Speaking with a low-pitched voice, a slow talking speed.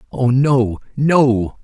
Yes: low, 130 Hz; slow, 110 wpm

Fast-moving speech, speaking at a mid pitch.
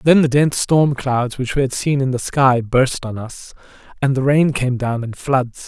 No: fast, 235 wpm; low, 130 Hz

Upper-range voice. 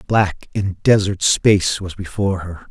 No: very low, 95 Hz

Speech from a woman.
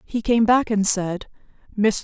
Yes: female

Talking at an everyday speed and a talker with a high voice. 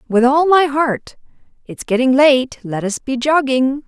Yes: average, 170 wpm; very high, 265 Hz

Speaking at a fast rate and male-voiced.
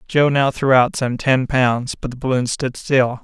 Yes: fast, 225 wpm; male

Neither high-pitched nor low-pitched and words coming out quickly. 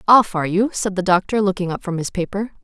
No: high, 195 Hz; fast, 250 wpm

